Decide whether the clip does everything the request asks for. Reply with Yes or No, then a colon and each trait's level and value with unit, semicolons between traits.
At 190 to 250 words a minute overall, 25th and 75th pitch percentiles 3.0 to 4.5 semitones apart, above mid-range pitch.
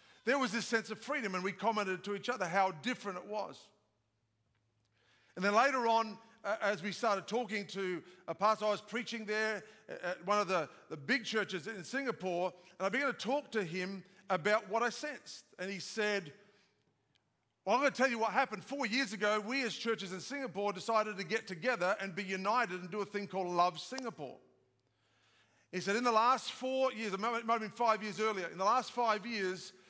Yes: fast, 205 wpm; average, 3.7 semitones; high, 205 Hz